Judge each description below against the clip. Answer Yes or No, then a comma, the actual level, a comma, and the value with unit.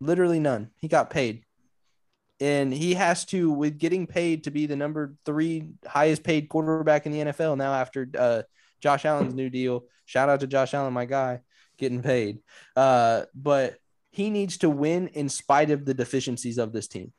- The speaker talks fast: No, average, 185 wpm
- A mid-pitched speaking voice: Yes, medium, 145 Hz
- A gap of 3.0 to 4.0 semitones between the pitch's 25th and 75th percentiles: Yes, average, 3.5 semitones